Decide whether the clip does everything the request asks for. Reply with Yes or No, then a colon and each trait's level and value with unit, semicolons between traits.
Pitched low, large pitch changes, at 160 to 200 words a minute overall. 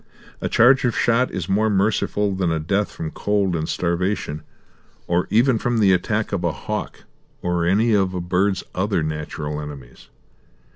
No: very low, 95 Hz; average, 3.6 semitones; average, 165 wpm